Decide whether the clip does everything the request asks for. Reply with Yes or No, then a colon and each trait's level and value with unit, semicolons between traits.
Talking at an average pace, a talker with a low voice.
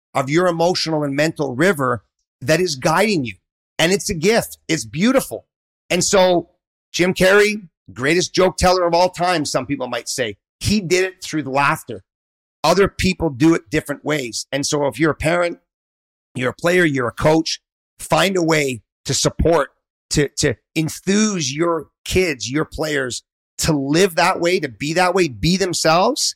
No: average, 175 wpm; medium, 160 Hz